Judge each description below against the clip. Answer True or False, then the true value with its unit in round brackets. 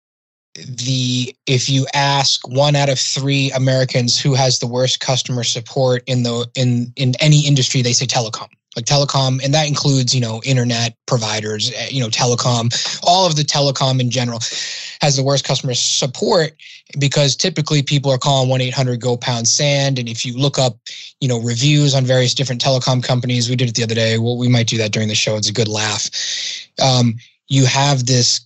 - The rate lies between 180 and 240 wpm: True (195 wpm)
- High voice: False (130 Hz)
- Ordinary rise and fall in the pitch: False (2.3 semitones)